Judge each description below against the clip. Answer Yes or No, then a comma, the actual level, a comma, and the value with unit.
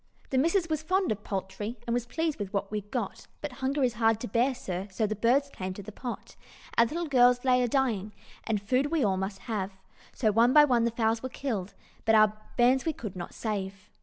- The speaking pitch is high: Yes, high, 235 Hz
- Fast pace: Yes, fast, 230 wpm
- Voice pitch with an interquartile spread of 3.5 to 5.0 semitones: Yes, average, 4.2 semitones